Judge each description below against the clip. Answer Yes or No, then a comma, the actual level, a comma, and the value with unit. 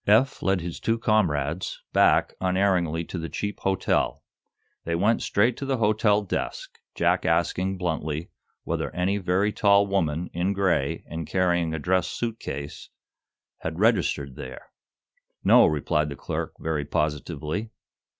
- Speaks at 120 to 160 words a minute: Yes, average, 140 wpm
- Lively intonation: No, average, 4.1 semitones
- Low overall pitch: Yes, very low, 90 Hz